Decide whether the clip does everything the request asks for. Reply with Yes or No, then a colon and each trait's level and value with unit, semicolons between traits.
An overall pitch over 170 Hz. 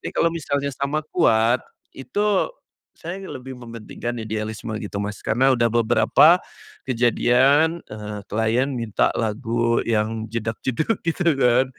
No: low, 120 Hz